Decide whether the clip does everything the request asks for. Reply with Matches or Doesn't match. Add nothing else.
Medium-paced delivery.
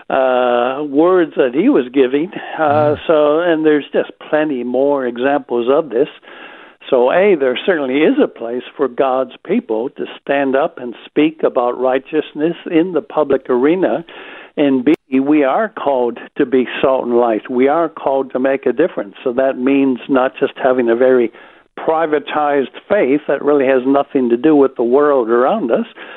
Matches